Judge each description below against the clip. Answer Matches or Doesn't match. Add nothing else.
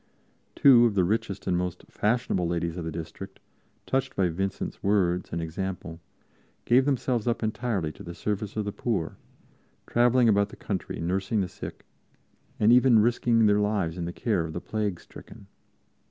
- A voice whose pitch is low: Matches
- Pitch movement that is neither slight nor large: Matches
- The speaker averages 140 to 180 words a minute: Matches